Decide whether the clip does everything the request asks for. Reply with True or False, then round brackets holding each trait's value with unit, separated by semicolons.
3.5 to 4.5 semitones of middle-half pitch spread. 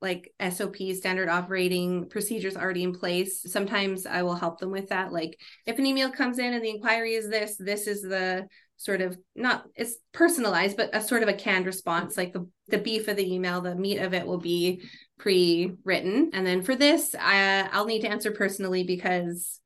False (2.8 semitones)